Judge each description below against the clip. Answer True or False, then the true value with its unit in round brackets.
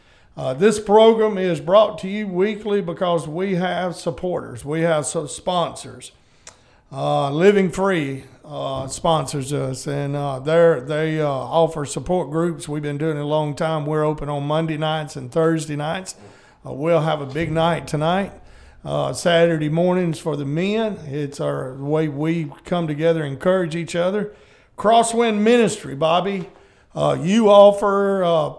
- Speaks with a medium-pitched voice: True (165 Hz)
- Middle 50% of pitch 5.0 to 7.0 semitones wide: False (3.7 semitones)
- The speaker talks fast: False (155 wpm)